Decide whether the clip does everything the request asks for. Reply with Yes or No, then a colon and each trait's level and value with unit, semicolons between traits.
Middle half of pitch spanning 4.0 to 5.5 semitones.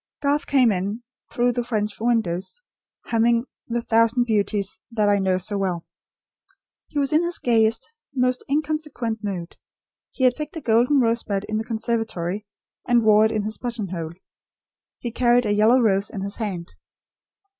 No: average, 3.1 semitones